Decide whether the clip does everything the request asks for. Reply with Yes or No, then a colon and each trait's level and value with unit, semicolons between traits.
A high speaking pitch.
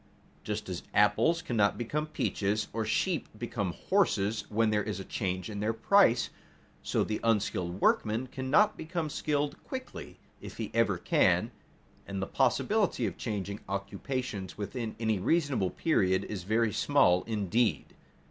No: low, 110 Hz